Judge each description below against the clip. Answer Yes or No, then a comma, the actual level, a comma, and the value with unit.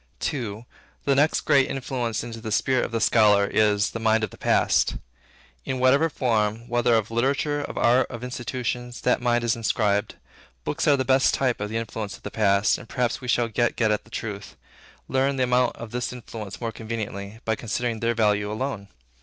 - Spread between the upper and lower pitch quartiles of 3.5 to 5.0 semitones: No, narrow, 2.6 semitones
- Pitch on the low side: Yes, low, 115 Hz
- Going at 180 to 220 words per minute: Yes, average, 195 wpm